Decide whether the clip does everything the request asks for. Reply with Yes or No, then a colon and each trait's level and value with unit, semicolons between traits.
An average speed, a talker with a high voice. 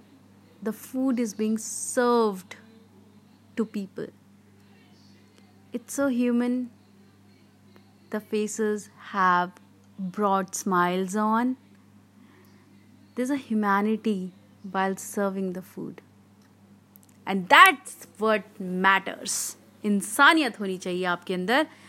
No: slow, 90 wpm; high, 195 Hz